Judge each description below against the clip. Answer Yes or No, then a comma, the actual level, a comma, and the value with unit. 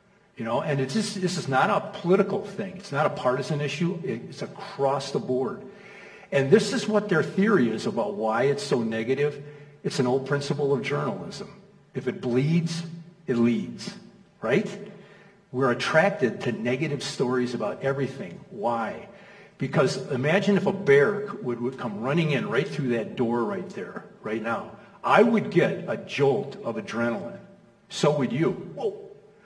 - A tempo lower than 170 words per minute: Yes, average, 160 wpm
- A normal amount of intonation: No, wide, 6.1 semitones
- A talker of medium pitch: No, high, 195 Hz